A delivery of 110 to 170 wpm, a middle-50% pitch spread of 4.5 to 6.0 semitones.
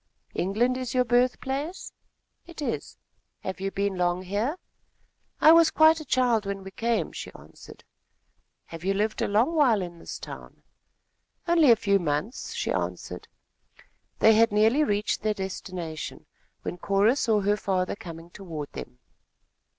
Yes: average, 155 wpm; average, 5.0 semitones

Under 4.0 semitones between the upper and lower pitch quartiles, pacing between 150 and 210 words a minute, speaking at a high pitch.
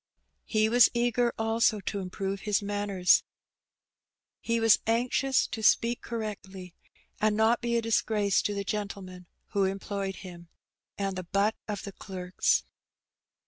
No: average, 2.7 semitones; average, 140 wpm; high, 205 Hz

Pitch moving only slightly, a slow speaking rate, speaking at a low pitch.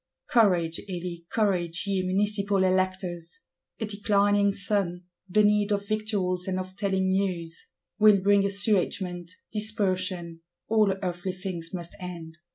No: narrow, 2.3 semitones; slow, 125 wpm; high, 190 Hz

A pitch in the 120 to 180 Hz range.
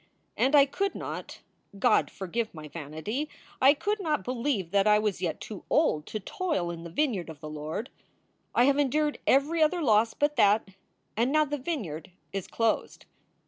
No: high, 230 Hz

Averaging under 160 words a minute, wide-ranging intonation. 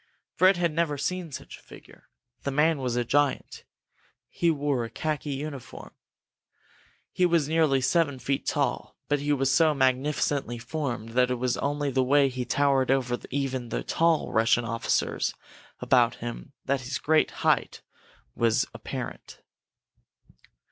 No: average, 150 wpm; average, 3.0 semitones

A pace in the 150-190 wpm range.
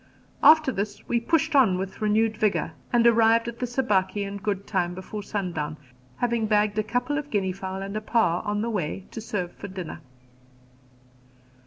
Yes: average, 180 wpm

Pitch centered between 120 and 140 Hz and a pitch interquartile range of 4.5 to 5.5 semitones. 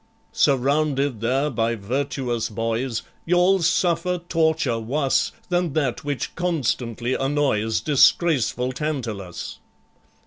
Yes: low, 135 Hz; average, 5.1 semitones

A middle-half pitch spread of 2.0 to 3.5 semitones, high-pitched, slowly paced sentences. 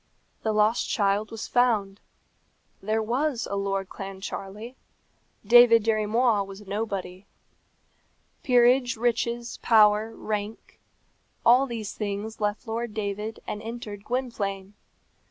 Yes: average, 2.7 semitones; high, 215 Hz; slow, 110 wpm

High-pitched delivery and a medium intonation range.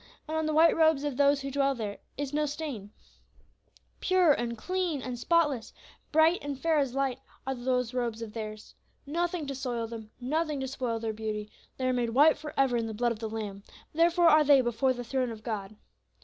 Yes: very high, 265 Hz; average, 4.6 semitones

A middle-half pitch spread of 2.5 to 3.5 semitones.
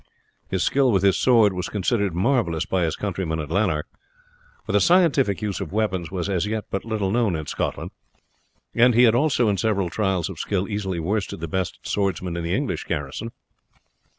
No: average, 3.9 semitones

